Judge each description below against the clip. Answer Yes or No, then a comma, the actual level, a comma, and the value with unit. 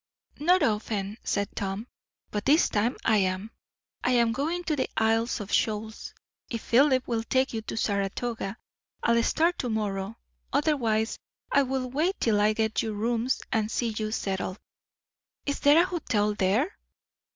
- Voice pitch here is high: Yes, high, 225 Hz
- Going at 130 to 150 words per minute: No, average, 160 wpm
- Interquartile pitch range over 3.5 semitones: Yes, average, 4.0 semitones